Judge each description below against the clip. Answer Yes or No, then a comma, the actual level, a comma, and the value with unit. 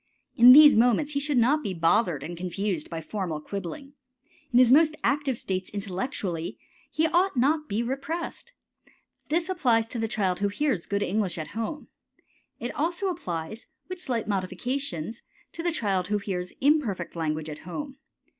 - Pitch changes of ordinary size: No, wide, 7.8 semitones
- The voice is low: No, high, 225 Hz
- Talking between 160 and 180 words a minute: Yes, average, 165 wpm